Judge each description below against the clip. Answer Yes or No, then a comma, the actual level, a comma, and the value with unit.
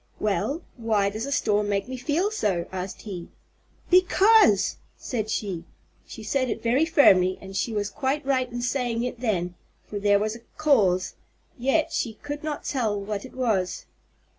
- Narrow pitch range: No, average, 5.2 semitones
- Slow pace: No, average, 170 wpm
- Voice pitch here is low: No, high, 230 Hz